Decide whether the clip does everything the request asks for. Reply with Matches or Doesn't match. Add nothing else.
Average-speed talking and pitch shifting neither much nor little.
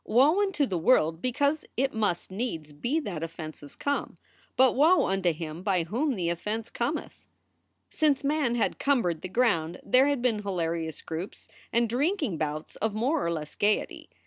Doesn't match